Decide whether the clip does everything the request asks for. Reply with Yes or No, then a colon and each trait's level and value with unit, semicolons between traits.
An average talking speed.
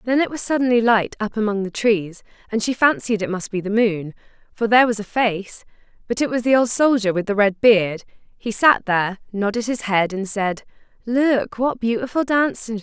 No: fast, 210 wpm